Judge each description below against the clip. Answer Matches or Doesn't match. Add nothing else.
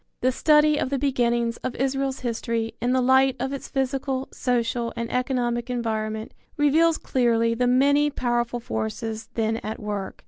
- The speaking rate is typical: Matches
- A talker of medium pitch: Doesn't match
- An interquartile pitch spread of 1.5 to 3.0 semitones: Matches